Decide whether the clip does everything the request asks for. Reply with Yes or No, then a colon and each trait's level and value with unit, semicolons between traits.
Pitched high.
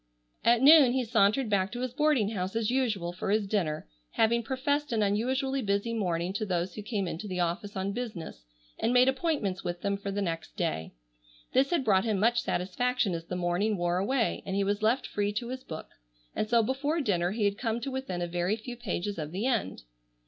Yes: high, 210 Hz